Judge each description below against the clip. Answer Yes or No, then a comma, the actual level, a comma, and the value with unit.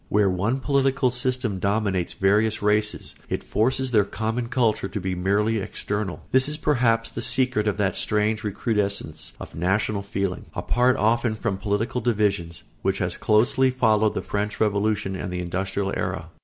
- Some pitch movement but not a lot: Yes, average, 3.1 semitones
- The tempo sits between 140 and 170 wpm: Yes, average, 160 wpm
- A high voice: No, low, 105 Hz